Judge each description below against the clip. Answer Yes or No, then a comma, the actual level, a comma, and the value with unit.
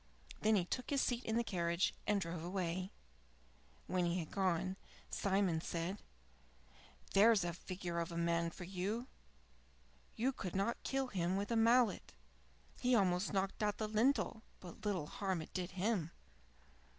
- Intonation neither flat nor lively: Yes, average, 3.9 semitones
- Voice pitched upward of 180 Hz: Yes, high, 190 Hz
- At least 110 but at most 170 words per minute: Yes, average, 160 wpm